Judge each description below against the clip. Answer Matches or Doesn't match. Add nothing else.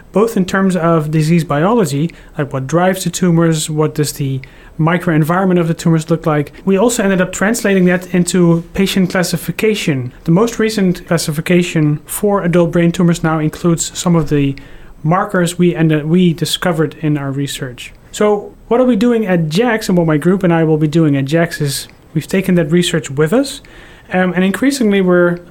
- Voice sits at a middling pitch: Matches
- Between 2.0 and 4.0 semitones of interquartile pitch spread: Matches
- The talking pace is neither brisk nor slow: Matches